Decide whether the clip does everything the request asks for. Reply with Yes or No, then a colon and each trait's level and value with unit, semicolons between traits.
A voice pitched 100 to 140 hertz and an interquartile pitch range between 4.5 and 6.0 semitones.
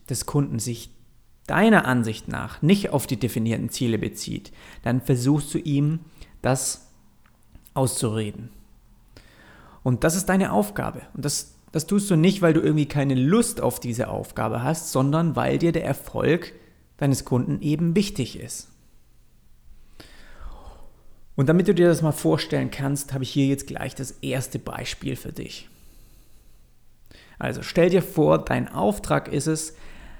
Yes: low, 135 Hz; average, 4.8 semitones